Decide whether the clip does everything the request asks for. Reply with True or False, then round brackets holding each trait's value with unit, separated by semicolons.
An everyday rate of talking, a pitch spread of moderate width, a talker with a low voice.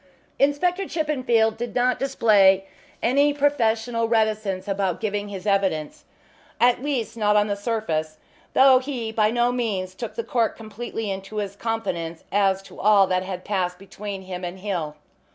False (155 wpm; 3.7 semitones; 215 Hz)